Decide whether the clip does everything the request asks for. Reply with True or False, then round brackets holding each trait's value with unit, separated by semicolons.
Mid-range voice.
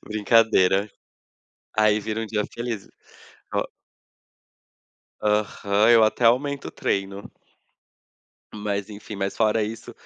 False (105 Hz)